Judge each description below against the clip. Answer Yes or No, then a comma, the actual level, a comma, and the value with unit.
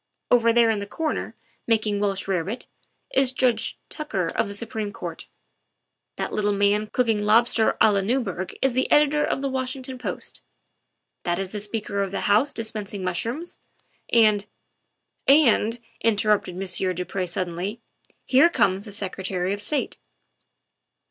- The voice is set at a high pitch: Yes, high, 210 Hz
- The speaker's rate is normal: Yes, average, 150 wpm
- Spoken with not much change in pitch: No, average, 3.6 semitones